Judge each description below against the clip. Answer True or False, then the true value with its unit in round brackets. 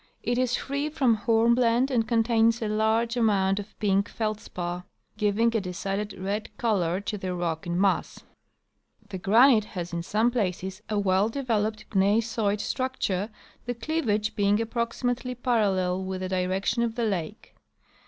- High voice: True (215 Hz)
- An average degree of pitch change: True (3.4 semitones)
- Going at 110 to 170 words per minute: True (155 wpm)